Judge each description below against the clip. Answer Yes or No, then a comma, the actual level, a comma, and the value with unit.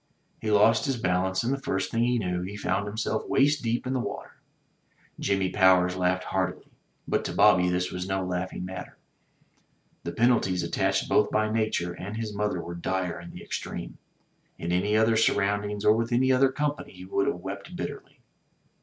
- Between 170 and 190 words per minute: Yes, average, 185 wpm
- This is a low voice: Yes, low, 100 Hz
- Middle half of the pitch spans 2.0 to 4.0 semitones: Yes, average, 3.6 semitones